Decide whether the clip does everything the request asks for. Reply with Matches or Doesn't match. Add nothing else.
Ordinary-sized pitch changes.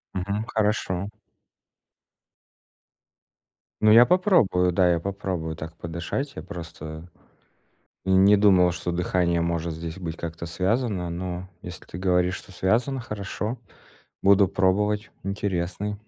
Matches